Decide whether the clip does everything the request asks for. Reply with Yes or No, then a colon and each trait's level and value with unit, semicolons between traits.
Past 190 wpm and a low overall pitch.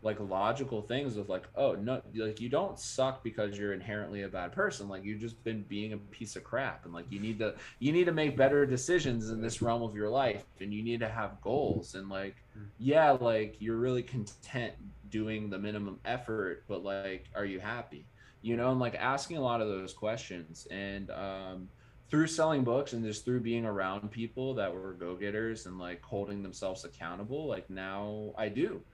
Yes: fast, 205 wpm; low, 110 Hz